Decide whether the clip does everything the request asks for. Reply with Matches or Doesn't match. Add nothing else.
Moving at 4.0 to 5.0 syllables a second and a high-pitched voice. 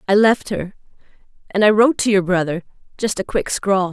Doesn't match